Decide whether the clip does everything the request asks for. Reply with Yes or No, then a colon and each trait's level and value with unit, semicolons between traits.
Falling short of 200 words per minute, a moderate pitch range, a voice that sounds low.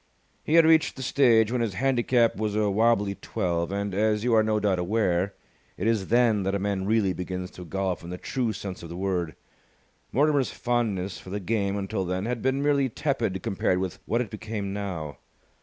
No: fast, 205 wpm; average, 3.7 semitones; low, 105 Hz